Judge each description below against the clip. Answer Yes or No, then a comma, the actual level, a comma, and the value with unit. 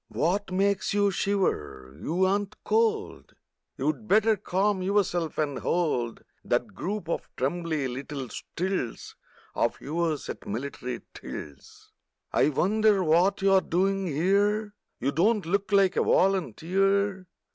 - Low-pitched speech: No, high, 190 Hz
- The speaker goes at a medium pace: No, slow, 125 wpm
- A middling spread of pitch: Yes, average, 4.3 semitones